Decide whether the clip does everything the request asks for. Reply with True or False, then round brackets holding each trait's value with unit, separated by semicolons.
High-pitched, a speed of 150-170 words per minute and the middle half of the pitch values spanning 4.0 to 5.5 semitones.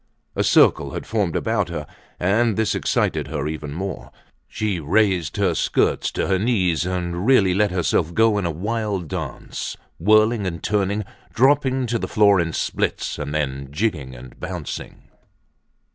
False (95 Hz; 160 wpm; 4.6 semitones)